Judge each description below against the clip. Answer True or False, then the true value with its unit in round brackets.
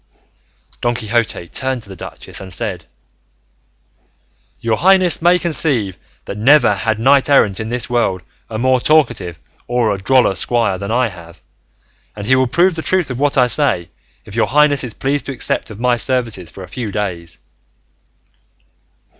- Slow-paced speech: False (170 wpm)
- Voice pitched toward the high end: False (120 Hz)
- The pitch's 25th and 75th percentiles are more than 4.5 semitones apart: True (5.1 semitones)